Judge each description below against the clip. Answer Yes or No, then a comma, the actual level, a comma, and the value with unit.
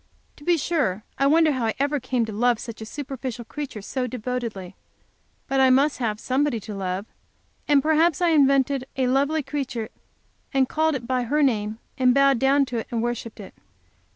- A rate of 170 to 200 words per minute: Yes, average, 190 wpm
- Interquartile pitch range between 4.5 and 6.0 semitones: No, average, 3.6 semitones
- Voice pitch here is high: Yes, very high, 260 Hz